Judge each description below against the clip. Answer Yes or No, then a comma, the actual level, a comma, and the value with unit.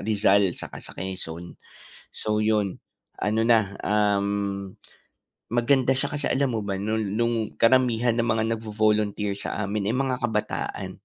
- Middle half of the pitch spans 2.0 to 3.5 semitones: Yes, average, 2.7 semitones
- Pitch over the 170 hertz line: No, low, 105 Hz